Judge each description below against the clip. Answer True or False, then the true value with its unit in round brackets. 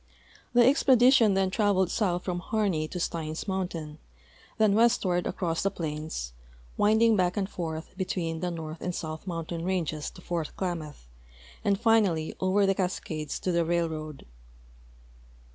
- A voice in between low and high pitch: True (180 Hz)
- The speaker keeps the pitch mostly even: False (3.7 semitones)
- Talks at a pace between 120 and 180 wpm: True (145 wpm)